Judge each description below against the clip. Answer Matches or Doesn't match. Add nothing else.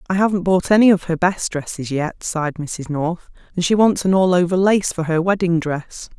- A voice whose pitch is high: Doesn't match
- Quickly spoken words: Matches